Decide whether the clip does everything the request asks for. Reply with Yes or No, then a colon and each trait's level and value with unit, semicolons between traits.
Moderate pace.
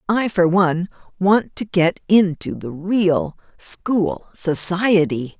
No: slow, 120 wpm